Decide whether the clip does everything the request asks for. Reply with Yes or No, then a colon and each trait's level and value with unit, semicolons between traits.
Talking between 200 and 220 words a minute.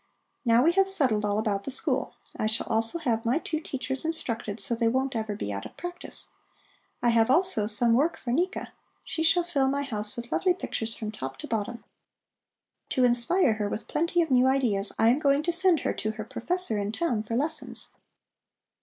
Yes: fast, 205 wpm